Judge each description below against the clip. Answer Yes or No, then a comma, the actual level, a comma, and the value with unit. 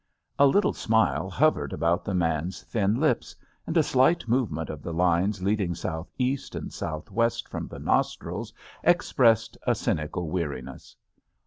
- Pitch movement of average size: No, wide, 6.8 semitones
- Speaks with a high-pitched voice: No, low, 100 Hz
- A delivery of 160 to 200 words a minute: No, average, 145 wpm